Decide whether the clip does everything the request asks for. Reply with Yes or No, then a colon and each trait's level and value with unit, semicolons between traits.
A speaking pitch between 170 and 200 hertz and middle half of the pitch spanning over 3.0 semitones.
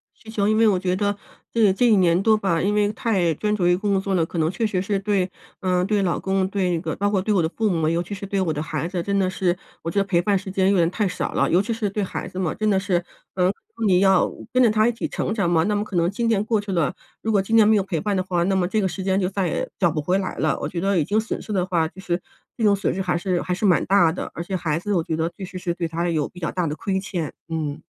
No: high, 190 Hz; average, 2.7 semitones